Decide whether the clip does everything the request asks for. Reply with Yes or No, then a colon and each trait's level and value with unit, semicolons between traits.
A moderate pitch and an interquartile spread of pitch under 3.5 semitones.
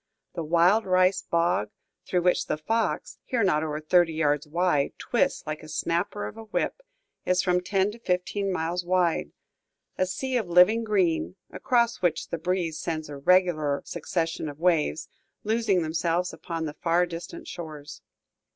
Yes: medium, 175 Hz; average, 2.8 semitones